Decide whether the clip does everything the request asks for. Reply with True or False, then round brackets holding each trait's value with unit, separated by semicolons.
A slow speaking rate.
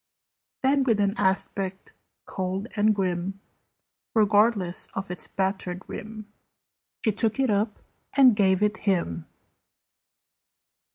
True (110 wpm)